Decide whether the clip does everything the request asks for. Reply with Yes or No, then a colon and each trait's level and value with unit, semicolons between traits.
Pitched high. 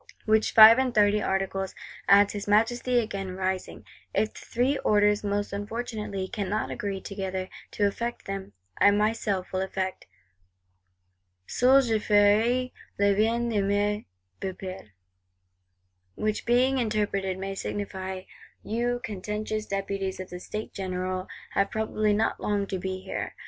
Yes: high, 205 Hz